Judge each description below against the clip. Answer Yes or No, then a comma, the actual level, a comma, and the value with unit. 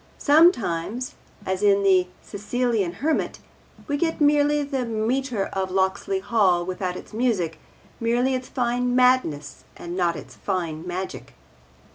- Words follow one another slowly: Yes, slow, 130 wpm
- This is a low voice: No, high, 215 Hz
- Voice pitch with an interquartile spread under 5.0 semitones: No, wide, 5.5 semitones